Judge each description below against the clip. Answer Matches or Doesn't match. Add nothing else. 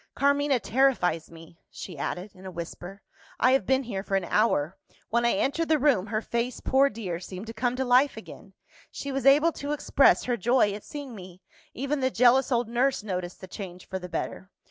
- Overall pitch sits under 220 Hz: Doesn't match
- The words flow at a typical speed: Doesn't match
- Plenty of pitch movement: Matches